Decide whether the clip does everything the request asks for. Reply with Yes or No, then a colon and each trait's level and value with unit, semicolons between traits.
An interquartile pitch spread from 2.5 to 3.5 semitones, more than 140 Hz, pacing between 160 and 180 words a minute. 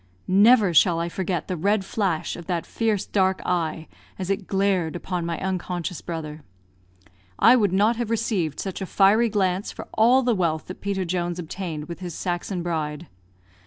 Yes: average, 2.9 semitones; medium, 185 Hz; average, 175 wpm